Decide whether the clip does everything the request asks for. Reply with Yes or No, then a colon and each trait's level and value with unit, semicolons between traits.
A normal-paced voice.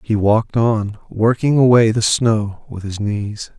Yes: average, 165 wpm